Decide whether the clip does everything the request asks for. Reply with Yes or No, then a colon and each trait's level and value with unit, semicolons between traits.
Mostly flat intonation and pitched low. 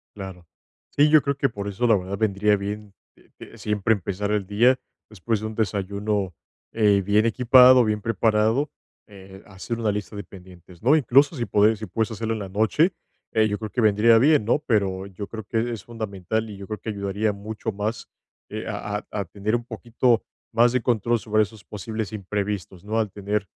Yes: narrow, 2.2 semitones; low, 105 Hz